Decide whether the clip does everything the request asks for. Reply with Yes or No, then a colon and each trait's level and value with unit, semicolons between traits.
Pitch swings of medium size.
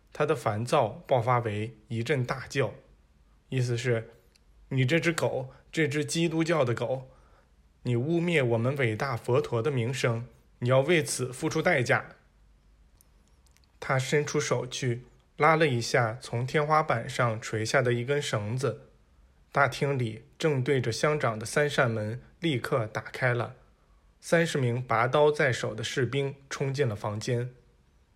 Yes: average, 4.6 semitones